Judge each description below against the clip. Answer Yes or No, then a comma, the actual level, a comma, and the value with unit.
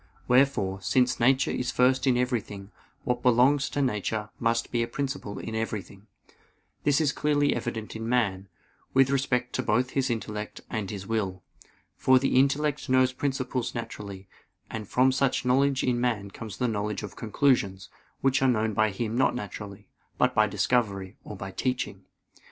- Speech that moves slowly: No, average, 165 wpm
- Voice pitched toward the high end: No, low, 120 Hz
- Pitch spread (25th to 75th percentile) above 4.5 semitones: No, average, 3.8 semitones